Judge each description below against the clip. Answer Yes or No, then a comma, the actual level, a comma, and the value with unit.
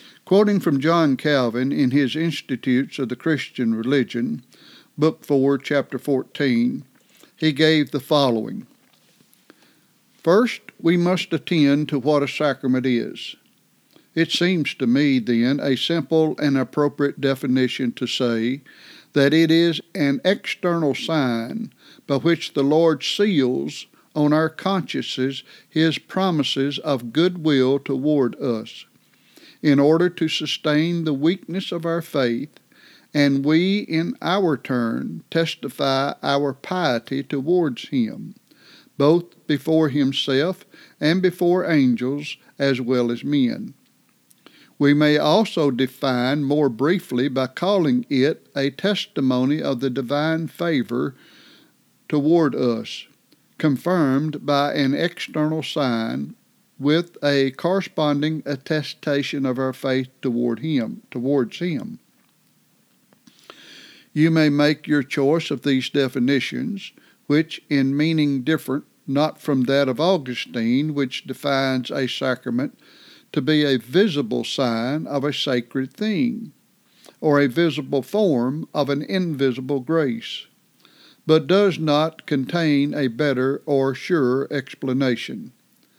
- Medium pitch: Yes, medium, 145 Hz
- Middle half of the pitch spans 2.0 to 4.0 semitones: Yes, average, 3.5 semitones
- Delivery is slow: Yes, slow, 120 wpm